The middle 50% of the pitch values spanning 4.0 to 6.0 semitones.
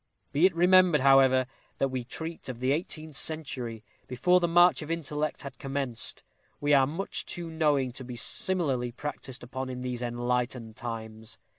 Yes: average, 4.3 semitones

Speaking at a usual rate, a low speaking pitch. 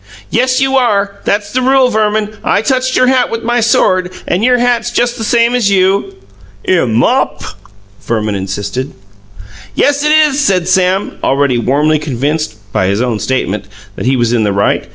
No: average, 175 wpm; high, 200 Hz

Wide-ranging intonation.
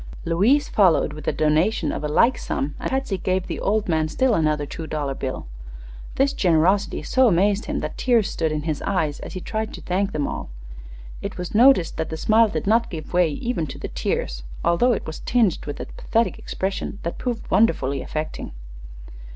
Yes: wide, 6.0 semitones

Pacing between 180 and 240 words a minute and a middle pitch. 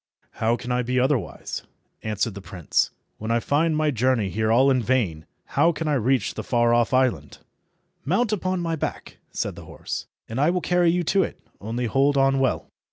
No: average, 200 wpm; low, 130 Hz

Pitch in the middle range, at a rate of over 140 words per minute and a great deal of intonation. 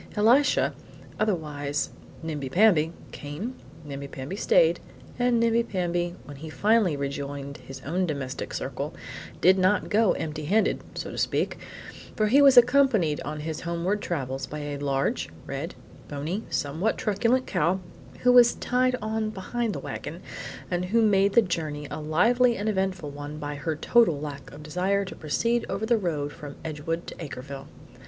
Yes: medium, 175 Hz; average, 160 wpm; wide, 6.8 semitones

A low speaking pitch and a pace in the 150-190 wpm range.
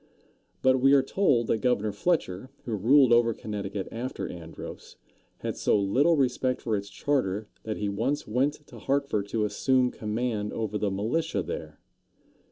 Yes: low, 115 Hz; average, 160 wpm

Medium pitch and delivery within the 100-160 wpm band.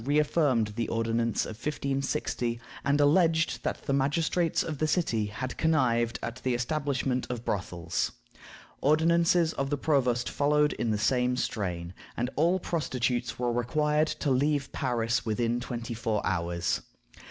No: low, 125 Hz; average, 140 wpm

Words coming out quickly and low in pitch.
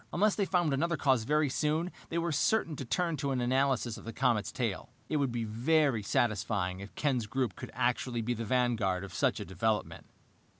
Yes: fast, 210 wpm; low, 125 Hz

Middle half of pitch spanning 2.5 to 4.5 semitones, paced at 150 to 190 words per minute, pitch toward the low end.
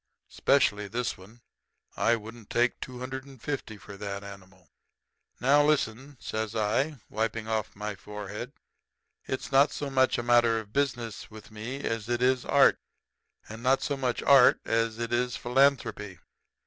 Yes: average, 3.6 semitones; average, 160 wpm; low, 115 Hz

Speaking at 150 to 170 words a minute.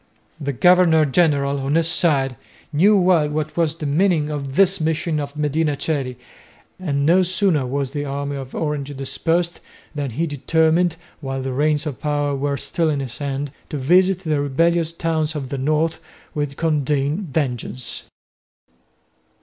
Yes: average, 160 wpm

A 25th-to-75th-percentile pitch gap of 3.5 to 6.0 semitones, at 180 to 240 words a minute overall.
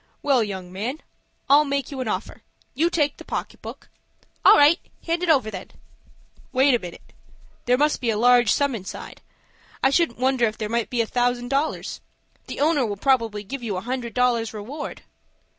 Yes: average, 4.1 semitones; average, 190 wpm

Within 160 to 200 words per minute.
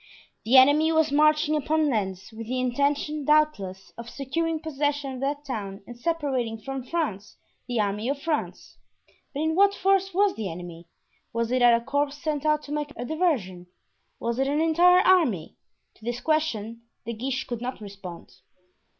Yes: average, 170 wpm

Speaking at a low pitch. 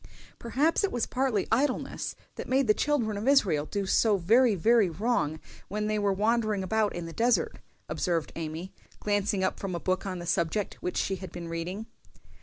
No: high, 205 Hz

